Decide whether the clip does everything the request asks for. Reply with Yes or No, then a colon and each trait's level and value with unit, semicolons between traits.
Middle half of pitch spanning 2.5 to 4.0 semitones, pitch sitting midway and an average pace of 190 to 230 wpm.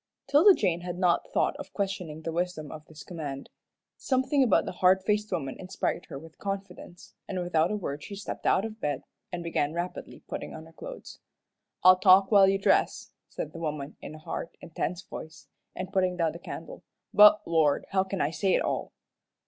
Yes: average, 3.5 semitones; medium, 180 Hz; average, 200 wpm